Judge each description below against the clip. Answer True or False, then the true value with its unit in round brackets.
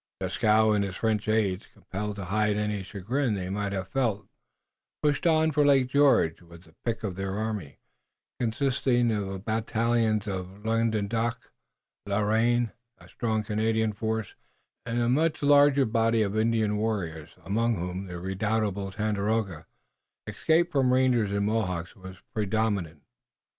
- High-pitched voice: False (110 Hz)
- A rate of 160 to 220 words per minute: False (150 wpm)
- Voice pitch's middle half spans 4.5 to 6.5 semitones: False (2.8 semitones)